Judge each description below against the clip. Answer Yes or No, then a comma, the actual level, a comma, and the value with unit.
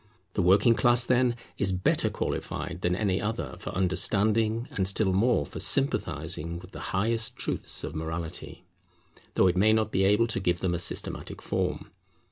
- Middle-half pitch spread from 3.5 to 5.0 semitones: Yes, average, 3.9 semitones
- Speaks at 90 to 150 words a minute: No, average, 170 wpm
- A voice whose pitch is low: Yes, very low, 95 Hz